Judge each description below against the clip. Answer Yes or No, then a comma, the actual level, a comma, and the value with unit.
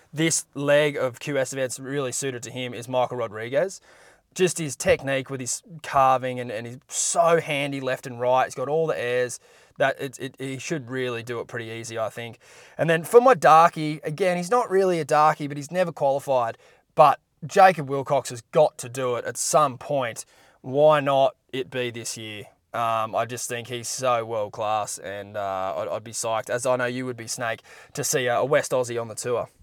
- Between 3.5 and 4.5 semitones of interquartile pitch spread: Yes, average, 4.0 semitones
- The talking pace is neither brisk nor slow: No, fast, 210 wpm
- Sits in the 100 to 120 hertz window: No, low, 130 Hz